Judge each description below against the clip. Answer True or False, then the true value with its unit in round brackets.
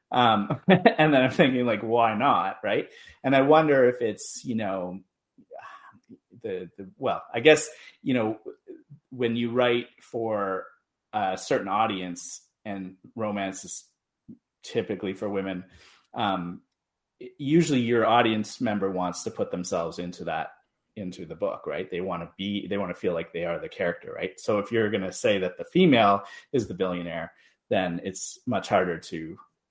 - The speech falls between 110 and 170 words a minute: True (165 wpm)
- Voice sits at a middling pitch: False (110 Hz)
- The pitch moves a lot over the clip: True (6.8 semitones)